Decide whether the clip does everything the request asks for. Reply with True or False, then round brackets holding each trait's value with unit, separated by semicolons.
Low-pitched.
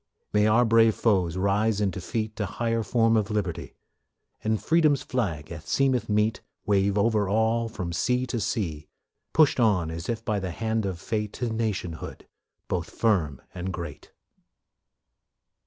True (105 Hz)